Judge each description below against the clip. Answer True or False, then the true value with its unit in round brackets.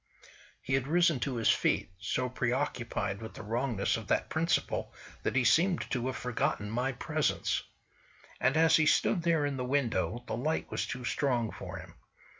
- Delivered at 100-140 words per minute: False (180 wpm)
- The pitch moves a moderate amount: True (3.7 semitones)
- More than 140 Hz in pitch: False (125 Hz)